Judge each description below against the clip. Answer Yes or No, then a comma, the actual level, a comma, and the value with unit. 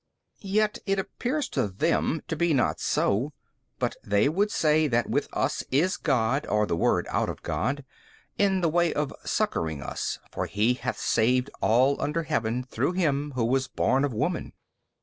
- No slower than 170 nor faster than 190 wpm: Yes, average, 180 wpm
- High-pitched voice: No, medium, 140 Hz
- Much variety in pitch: Yes, wide, 5.8 semitones